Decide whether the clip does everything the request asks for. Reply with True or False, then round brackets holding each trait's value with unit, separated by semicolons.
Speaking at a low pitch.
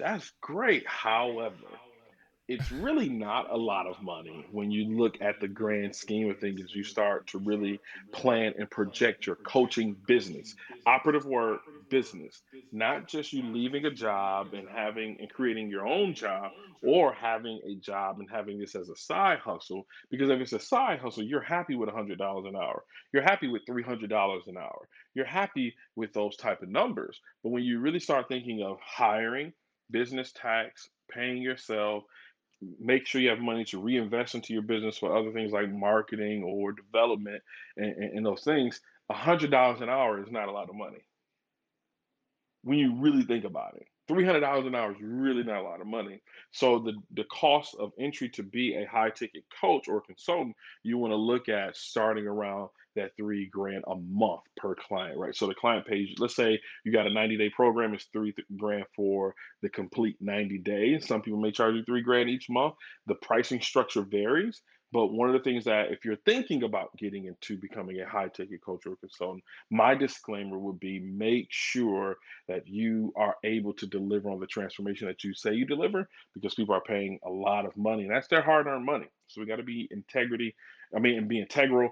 True (110 Hz)